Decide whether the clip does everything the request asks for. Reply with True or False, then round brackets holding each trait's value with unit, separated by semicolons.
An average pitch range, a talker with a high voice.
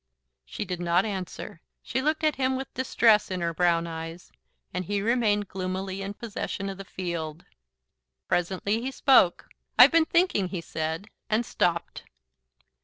True (4.9 semitones; 195 Hz)